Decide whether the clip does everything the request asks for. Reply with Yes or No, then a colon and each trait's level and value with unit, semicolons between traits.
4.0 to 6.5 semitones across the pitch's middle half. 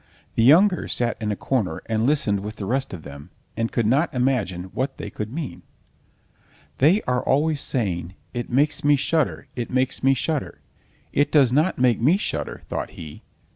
Yes: average, 5.1 semitones